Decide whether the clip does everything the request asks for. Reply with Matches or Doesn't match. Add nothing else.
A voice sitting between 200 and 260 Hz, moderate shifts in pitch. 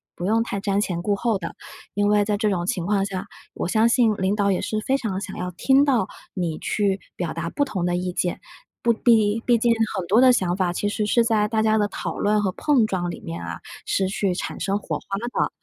Matches